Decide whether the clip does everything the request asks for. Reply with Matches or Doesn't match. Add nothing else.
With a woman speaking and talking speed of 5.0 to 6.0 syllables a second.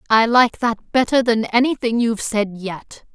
Doesn't match